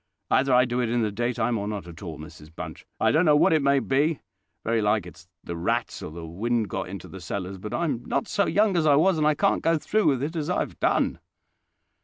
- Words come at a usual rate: No, fast, 255 wpm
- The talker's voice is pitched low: Yes, low, 120 Hz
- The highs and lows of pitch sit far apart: Yes, wide, 7.5 semitones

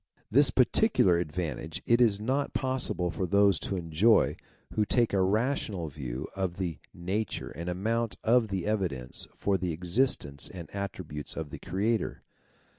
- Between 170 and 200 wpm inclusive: No, average, 150 wpm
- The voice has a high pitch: No, very low, 95 Hz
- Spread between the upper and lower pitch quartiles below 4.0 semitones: No, average, 4.7 semitones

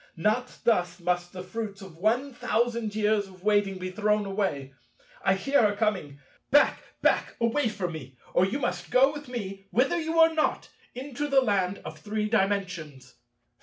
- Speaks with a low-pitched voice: No, high, 205 Hz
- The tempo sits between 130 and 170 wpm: Yes, average, 165 wpm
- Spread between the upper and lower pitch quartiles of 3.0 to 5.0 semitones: Yes, average, 4.7 semitones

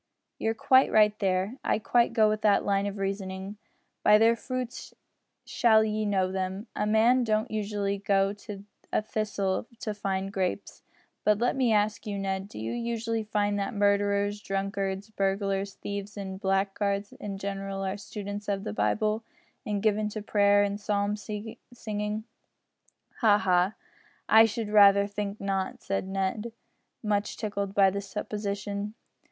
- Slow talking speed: No, average, 155 wpm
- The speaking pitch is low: No, high, 205 Hz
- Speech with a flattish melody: Yes, narrow, 1.5 semitones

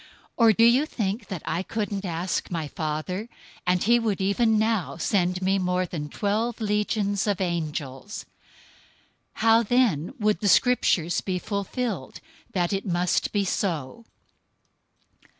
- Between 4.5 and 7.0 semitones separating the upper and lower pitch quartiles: No, average, 3.8 semitones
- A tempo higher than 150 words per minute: No, average, 145 wpm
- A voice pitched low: No, high, 195 Hz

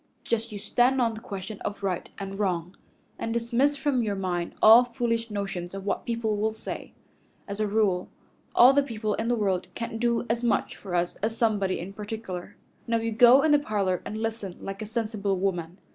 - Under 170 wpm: No, fast, 205 wpm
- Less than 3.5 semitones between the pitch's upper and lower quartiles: Yes, average, 3.0 semitones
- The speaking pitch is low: No, high, 215 Hz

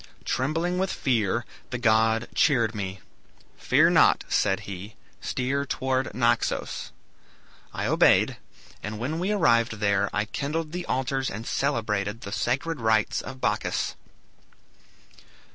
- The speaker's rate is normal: No, slow, 125 wpm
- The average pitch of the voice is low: Yes, low, 120 Hz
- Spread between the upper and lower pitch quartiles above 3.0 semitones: Yes, average, 4.5 semitones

